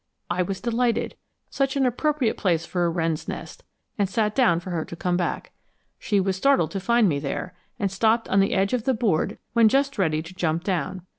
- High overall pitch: Yes, high, 195 Hz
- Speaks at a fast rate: Yes, fast, 215 wpm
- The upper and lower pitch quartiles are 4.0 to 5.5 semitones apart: Yes, average, 5.2 semitones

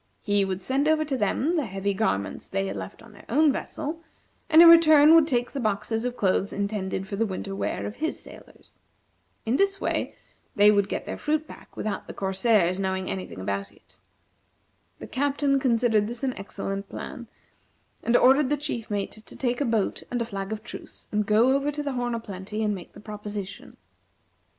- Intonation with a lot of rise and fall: Yes, wide, 5.8 semitones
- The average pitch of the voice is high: Yes, high, 220 Hz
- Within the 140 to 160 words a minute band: No, fast, 205 wpm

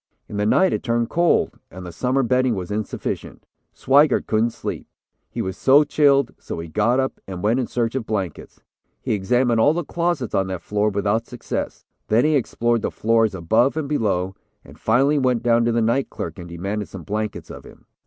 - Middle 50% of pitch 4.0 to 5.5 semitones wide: Yes, average, 4.3 semitones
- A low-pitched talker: Yes, low, 115 Hz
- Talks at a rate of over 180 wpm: Yes, fast, 205 wpm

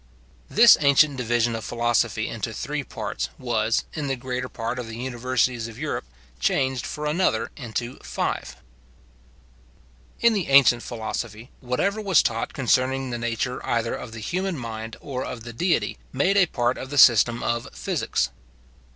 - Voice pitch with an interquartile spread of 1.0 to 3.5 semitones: Yes, average, 3.1 semitones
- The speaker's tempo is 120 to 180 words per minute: Yes, average, 160 wpm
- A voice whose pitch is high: No, low, 125 Hz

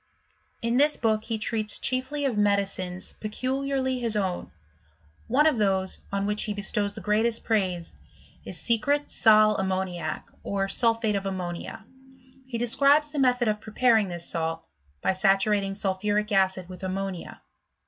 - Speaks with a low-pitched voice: No, high, 210 Hz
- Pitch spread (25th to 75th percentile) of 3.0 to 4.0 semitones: Yes, average, 3.6 semitones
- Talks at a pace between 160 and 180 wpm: No, average, 150 wpm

